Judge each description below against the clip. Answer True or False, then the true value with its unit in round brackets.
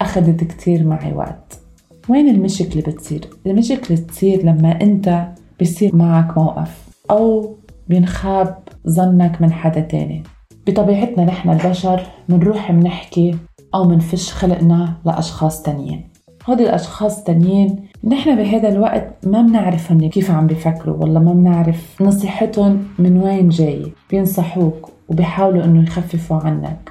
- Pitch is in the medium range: True (175 Hz)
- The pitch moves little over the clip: False (3.0 semitones)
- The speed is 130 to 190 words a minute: False (120 wpm)